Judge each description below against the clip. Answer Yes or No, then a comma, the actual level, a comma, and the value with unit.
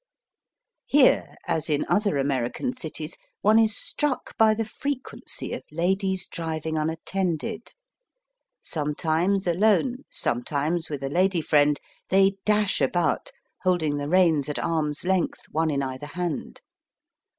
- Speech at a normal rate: No, slow, 125 wpm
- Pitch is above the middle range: No, medium, 170 Hz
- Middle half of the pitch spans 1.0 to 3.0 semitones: No, average, 4.7 semitones